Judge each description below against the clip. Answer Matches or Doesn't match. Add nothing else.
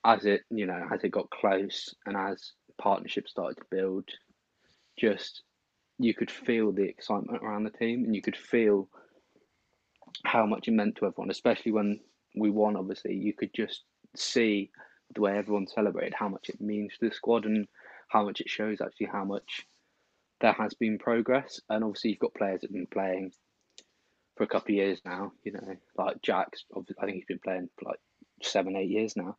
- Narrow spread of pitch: Matches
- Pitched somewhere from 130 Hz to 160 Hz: Doesn't match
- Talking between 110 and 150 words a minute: Doesn't match